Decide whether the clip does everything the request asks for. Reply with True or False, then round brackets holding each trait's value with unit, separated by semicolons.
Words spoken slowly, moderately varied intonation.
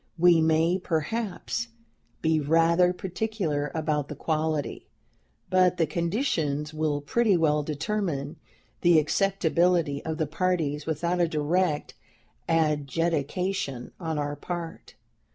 True (110 wpm; 3.1 semitones)